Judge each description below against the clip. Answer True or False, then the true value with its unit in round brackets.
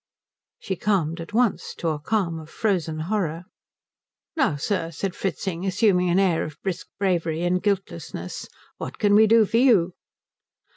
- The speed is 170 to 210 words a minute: False (155 wpm)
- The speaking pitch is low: False (180 Hz)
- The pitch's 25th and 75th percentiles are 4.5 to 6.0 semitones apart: False (3.8 semitones)